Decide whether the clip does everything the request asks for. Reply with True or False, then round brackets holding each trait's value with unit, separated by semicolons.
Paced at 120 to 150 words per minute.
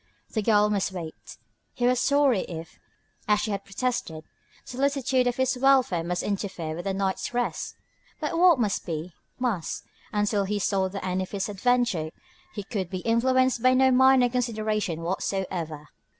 False (165 wpm)